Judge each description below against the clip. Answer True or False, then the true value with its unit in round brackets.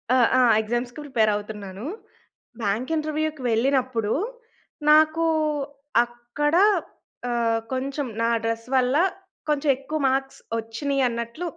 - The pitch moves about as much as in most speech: True (4.1 semitones)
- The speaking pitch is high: True (255 Hz)